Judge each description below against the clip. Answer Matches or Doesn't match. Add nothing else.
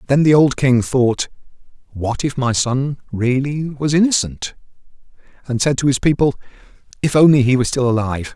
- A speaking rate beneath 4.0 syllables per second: Doesn't match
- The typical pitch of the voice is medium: Doesn't match